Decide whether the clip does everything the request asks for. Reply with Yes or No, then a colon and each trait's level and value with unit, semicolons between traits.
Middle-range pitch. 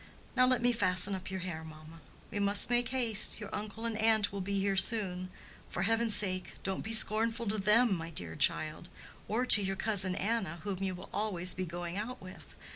No: high, 200 Hz